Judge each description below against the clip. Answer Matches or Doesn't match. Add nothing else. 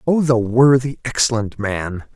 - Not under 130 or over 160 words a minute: Matches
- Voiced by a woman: Doesn't match